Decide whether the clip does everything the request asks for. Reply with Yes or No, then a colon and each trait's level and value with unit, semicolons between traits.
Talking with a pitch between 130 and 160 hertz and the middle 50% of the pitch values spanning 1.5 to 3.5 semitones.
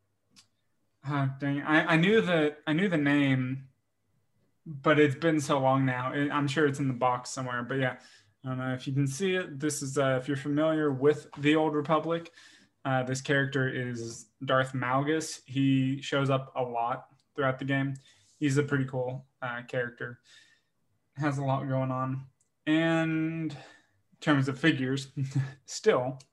Yes: low, 135 Hz; narrow, 2.5 semitones